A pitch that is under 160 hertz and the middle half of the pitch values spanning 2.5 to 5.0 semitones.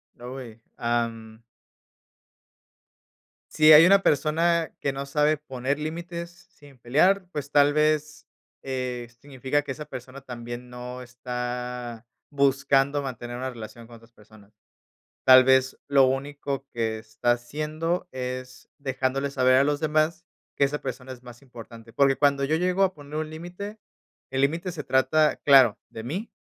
Yes: low, 135 Hz; average, 3.6 semitones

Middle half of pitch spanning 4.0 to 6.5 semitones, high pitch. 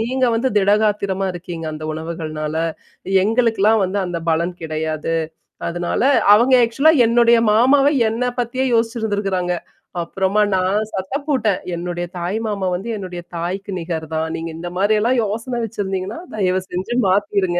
Yes: average, 4.3 semitones; high, 195 Hz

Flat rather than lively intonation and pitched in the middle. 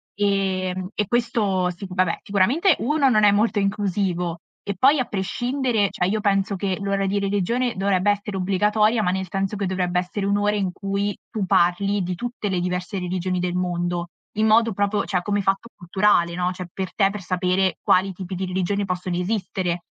No: narrow, 2.2 semitones; high, 195 Hz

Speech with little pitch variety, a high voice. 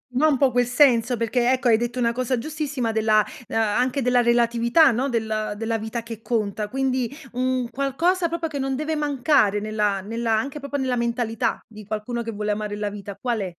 No: average, 3.2 semitones; high, 235 Hz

